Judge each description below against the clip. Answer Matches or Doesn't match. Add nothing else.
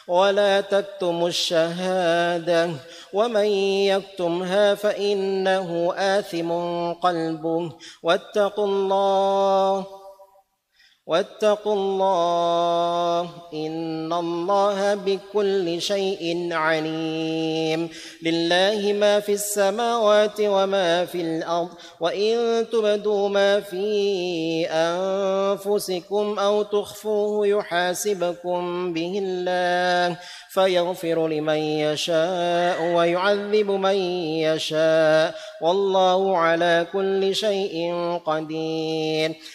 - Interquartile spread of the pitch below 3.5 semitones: Matches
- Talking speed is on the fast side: Doesn't match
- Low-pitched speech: Doesn't match